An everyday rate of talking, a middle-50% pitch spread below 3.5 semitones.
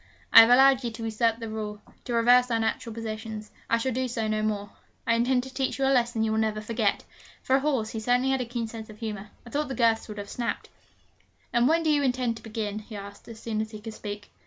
No: fast, 260 wpm; narrow, 2.4 semitones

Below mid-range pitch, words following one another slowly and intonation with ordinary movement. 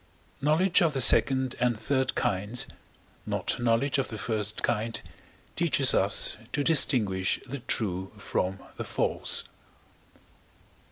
Yes: low, 120 Hz; slow, 120 wpm; average, 4.3 semitones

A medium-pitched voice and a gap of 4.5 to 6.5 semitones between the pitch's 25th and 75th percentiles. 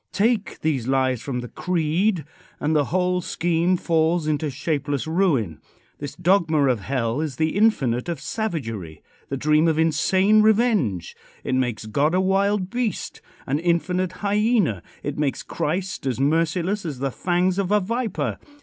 Yes: medium, 160 Hz; wide, 5.4 semitones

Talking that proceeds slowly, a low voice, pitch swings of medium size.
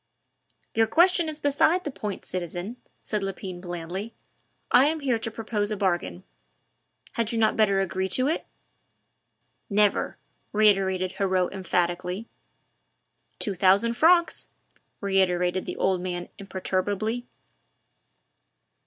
No: slow, 115 wpm; high, 200 Hz; average, 3.7 semitones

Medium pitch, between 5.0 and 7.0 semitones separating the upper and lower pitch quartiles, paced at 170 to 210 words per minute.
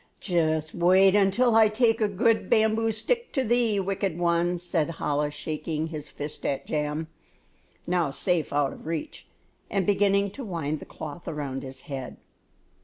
No: medium, 175 Hz; average, 5.3 semitones; average, 160 wpm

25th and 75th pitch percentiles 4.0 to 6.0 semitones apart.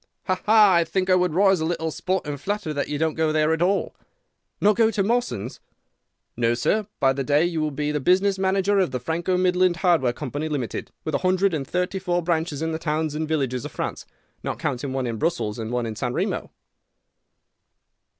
Yes: average, 4.4 semitones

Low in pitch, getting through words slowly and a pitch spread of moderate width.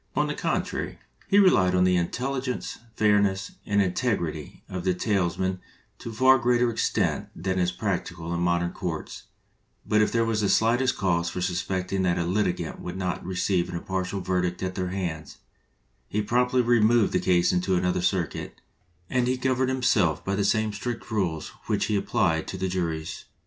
No: very low, 95 Hz; average, 180 wpm; average, 3.8 semitones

